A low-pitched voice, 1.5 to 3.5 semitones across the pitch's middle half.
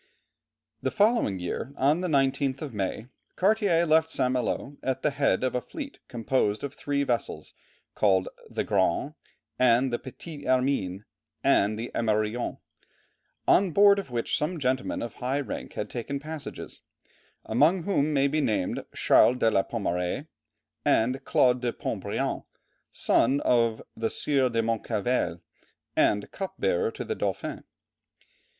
No: low, 130 Hz; average, 4.7 semitones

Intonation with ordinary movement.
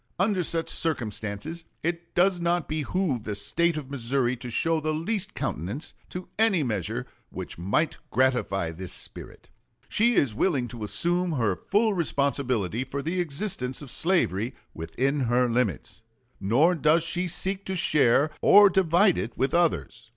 No: wide, 6.6 semitones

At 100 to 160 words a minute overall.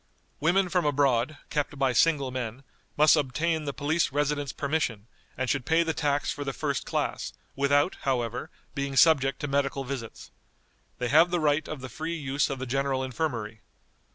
No: average, 175 wpm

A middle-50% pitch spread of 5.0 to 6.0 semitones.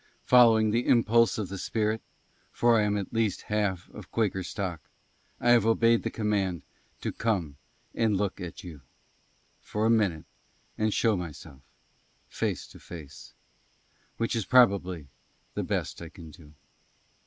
No: average, 4.2 semitones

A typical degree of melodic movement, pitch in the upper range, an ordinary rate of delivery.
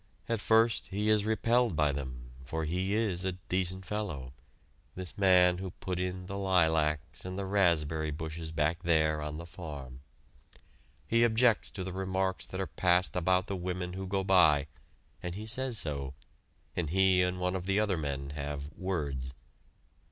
No: average, 3.7 semitones; very low, 90 Hz; average, 170 wpm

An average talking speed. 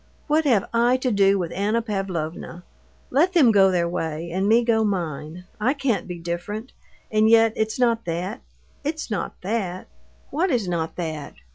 Yes: average, 170 wpm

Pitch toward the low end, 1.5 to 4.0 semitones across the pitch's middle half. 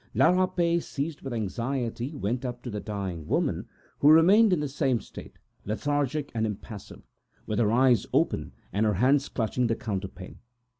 No: low, 125 Hz; average, 5.2 semitones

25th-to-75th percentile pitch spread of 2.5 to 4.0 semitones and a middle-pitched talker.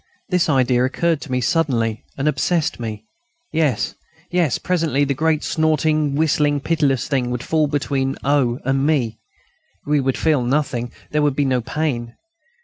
Yes: average, 3.5 semitones; medium, 145 Hz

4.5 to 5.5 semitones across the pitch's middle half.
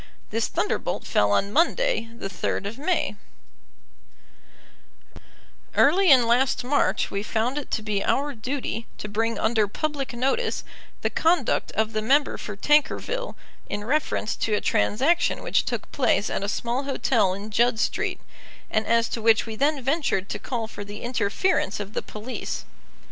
Yes: average, 5.0 semitones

